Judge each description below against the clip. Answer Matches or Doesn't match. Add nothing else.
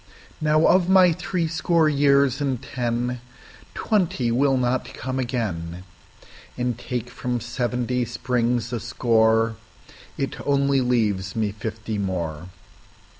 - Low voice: Matches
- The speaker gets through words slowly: Matches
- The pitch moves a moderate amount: Matches